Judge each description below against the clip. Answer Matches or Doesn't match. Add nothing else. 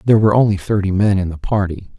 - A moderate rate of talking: Doesn't match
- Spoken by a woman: Doesn't match